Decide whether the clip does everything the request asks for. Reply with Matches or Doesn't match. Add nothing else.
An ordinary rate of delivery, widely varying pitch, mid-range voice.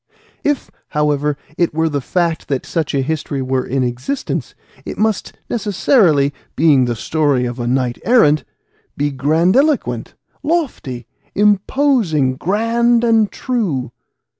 Doesn't match